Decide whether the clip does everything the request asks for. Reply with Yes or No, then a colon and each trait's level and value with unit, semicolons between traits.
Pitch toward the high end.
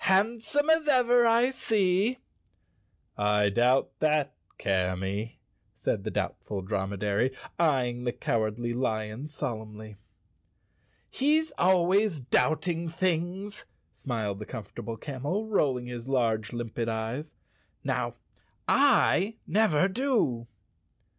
No: low, 135 Hz